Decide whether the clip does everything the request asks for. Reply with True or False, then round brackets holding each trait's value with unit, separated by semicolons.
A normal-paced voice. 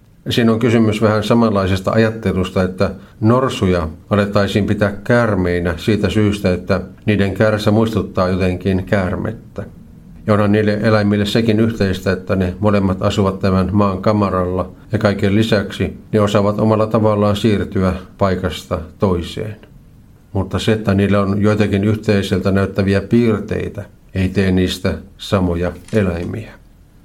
True (125 wpm)